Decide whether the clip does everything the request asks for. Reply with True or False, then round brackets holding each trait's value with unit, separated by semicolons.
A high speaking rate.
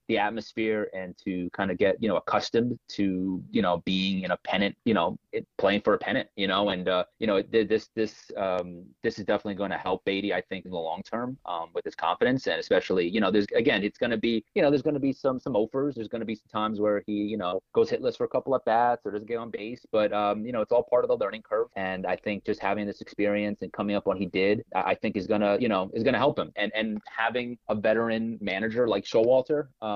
True (275 wpm)